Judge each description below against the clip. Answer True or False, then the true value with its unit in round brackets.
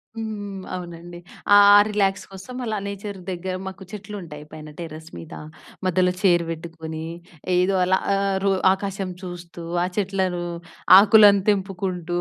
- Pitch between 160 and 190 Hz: True (185 Hz)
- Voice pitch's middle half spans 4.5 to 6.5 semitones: False (2.4 semitones)